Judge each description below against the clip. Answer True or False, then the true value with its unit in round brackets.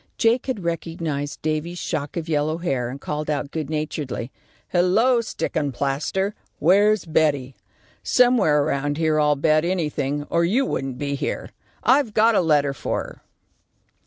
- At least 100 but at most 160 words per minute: True (150 wpm)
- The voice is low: False (155 Hz)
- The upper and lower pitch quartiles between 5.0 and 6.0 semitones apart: False (4.1 semitones)